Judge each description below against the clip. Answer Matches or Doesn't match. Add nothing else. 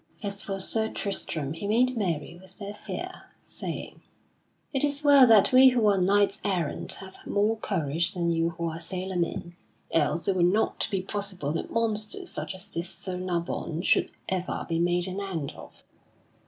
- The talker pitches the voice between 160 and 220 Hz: Matches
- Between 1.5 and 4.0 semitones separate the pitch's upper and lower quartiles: Matches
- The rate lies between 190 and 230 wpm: Doesn't match